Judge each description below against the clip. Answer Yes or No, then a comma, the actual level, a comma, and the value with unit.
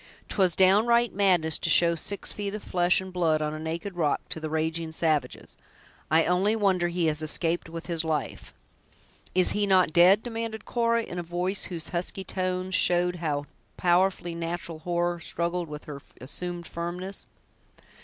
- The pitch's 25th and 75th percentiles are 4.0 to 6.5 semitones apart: No, narrow, 2.5 semitones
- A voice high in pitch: No, medium, 175 Hz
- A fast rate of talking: No, average, 165 wpm